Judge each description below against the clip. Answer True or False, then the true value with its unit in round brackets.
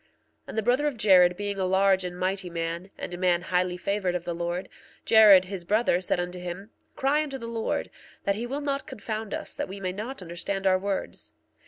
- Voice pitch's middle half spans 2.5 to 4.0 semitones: True (3.4 semitones)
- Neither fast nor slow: False (220 wpm)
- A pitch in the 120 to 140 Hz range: False (190 Hz)